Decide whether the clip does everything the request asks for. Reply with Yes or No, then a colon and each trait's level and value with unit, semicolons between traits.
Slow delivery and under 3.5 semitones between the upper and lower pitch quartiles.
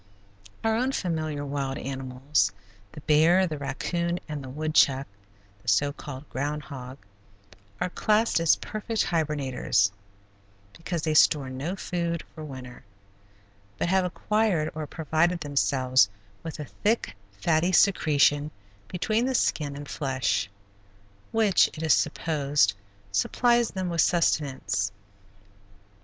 No: slow, 120 wpm; average, 4.2 semitones